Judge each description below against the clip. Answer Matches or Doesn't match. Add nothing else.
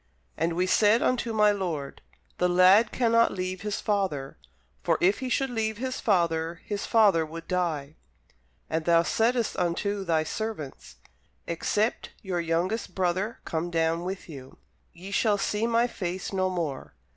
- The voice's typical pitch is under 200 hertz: Matches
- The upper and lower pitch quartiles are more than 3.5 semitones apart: Matches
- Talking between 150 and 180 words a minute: Matches